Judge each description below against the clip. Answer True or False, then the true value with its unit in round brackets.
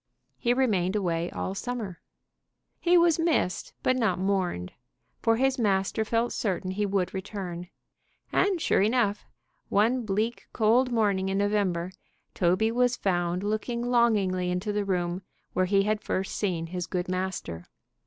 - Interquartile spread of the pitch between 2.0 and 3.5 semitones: False (4.1 semitones)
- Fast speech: False (145 wpm)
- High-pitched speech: True (200 Hz)